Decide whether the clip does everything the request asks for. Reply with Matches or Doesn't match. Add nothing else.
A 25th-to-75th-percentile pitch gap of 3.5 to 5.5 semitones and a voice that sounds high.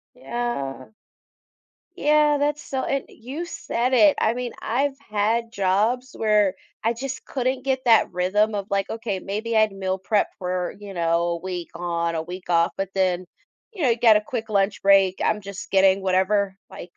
Matches